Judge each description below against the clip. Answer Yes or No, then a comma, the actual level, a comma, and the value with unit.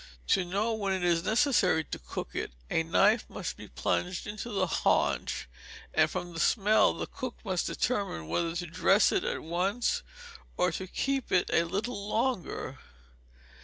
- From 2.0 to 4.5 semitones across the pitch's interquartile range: Yes, average, 3.9 semitones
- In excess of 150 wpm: Yes, average, 165 wpm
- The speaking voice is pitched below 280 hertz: Yes, high, 190 Hz